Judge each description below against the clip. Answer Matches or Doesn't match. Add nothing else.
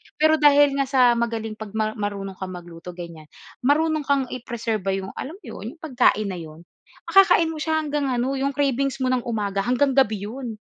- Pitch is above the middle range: Matches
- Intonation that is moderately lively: Doesn't match